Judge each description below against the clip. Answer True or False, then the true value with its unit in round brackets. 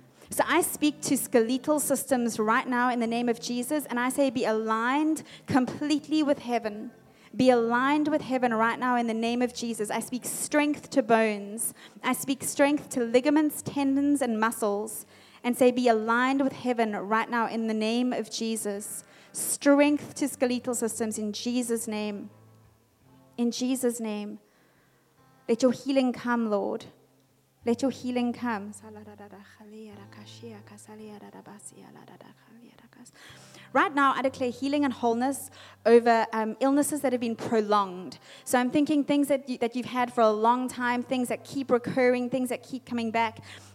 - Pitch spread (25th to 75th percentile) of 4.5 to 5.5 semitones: False (3.1 semitones)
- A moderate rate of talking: True (155 wpm)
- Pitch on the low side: False (240 Hz)